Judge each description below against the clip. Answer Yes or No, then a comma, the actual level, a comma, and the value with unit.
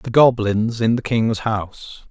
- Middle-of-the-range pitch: No, low, 110 Hz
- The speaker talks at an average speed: Yes, average, 170 wpm